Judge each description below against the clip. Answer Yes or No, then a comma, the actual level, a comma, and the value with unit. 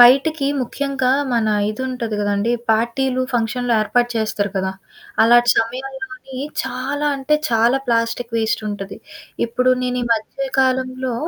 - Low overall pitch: No, high, 245 Hz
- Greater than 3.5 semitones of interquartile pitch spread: No, narrow, 2.6 semitones